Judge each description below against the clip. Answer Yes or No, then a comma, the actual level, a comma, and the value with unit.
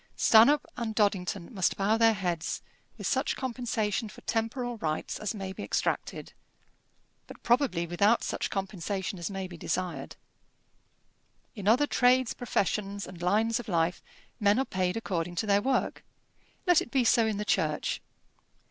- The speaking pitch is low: No, high, 205 Hz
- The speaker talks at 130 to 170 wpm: Yes, average, 155 wpm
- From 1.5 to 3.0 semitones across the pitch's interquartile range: No, average, 3.8 semitones